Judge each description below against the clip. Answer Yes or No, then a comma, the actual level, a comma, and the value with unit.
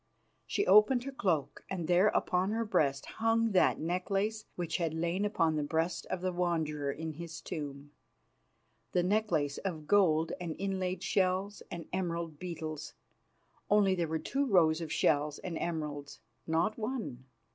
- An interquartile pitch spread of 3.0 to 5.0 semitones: Yes, average, 3.8 semitones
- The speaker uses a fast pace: No, average, 155 wpm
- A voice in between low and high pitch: Yes, medium, 175 Hz